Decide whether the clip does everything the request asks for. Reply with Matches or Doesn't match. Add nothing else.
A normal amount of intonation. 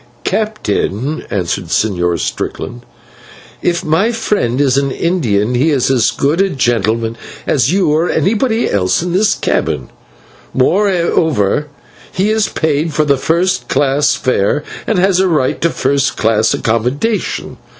Doesn't match